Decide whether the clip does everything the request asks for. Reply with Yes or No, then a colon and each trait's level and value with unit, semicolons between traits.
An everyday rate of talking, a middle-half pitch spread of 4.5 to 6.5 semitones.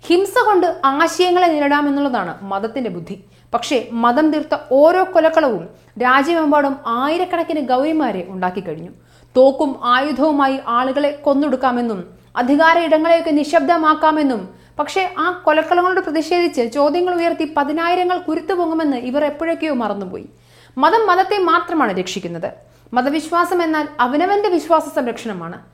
Yes: average, 100 wpm; average, 4.8 semitones